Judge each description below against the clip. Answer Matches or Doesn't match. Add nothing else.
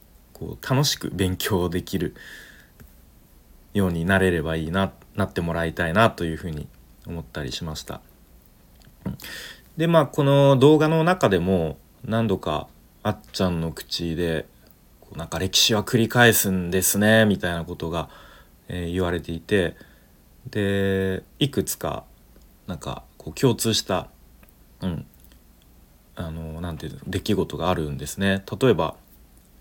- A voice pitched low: Matches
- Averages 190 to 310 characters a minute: Matches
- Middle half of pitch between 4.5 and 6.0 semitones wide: Doesn't match